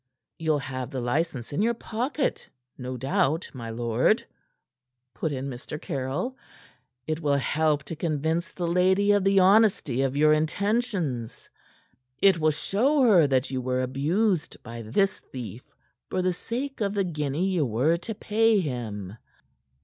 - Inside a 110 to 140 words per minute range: No, average, 150 wpm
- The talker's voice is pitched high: No, medium, 155 Hz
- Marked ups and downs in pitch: Yes, wide, 7.0 semitones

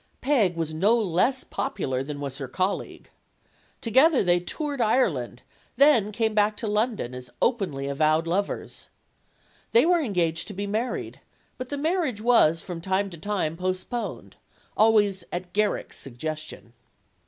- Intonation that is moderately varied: No, wide, 6.4 semitones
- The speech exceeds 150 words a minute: No, average, 140 wpm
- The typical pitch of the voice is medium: No, high, 200 Hz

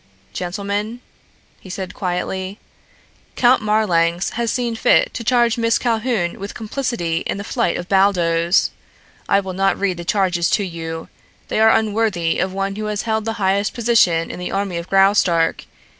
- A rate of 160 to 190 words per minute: Yes, average, 165 wpm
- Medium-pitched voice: No, high, 195 Hz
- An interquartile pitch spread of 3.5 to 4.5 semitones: Yes, average, 3.8 semitones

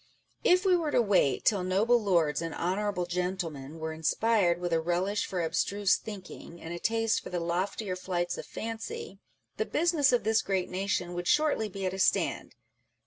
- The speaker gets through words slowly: No, average, 185 wpm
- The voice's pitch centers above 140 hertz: Yes, high, 190 Hz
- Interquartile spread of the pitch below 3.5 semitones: No, average, 4.0 semitones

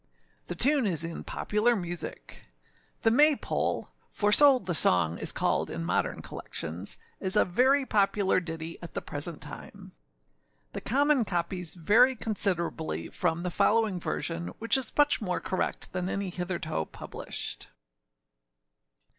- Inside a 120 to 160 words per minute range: Yes, average, 140 wpm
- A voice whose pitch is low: No, medium, 185 Hz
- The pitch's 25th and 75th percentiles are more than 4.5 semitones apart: Yes, average, 5.1 semitones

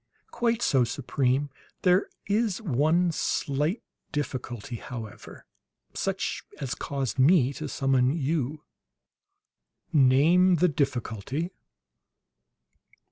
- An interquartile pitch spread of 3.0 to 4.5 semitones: No, average, 4.9 semitones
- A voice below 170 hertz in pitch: Yes, medium, 140 Hz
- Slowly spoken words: Yes, slow, 85 wpm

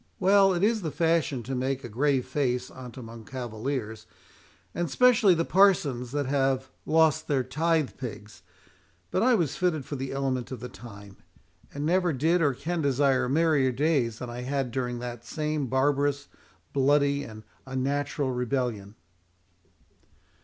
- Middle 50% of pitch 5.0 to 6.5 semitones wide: No, average, 3.9 semitones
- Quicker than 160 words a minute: No, average, 155 wpm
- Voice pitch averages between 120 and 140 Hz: Yes, low, 135 Hz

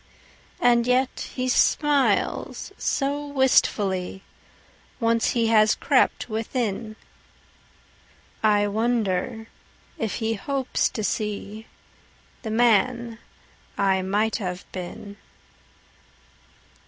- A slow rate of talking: Yes, slow, 75 wpm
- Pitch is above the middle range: Yes, high, 225 Hz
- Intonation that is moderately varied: Yes, average, 3.0 semitones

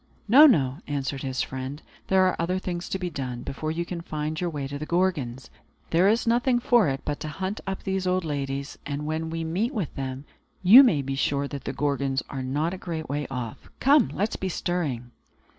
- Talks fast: Yes, fast, 220 wpm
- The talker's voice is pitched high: No, medium, 155 Hz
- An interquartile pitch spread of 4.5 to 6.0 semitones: Yes, average, 5.3 semitones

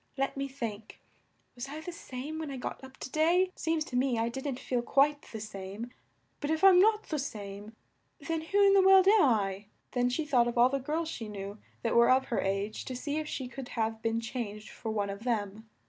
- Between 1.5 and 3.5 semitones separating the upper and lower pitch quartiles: No, wide, 5.6 semitones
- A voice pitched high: Yes, very high, 255 Hz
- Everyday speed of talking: No, fast, 230 wpm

